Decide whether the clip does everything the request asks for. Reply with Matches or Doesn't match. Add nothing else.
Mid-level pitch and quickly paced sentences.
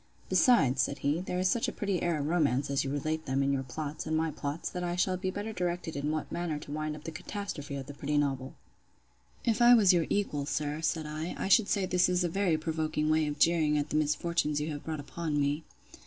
Matches